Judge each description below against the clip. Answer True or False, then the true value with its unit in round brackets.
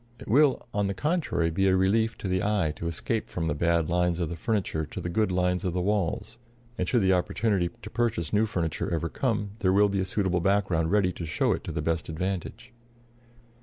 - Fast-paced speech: True (225 wpm)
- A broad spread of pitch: False (3.8 semitones)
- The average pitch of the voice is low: True (95 Hz)